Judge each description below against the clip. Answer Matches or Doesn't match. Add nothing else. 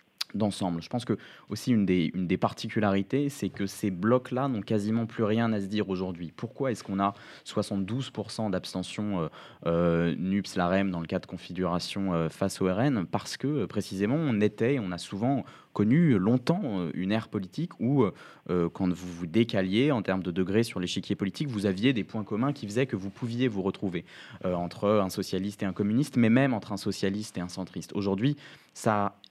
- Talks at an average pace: Matches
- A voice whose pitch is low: Matches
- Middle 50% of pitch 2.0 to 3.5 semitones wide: Matches